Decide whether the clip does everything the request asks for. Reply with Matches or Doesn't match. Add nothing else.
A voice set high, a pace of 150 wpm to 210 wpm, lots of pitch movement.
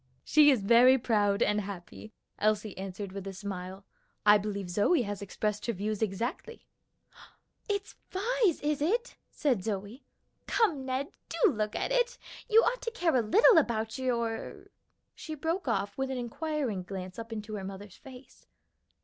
Matches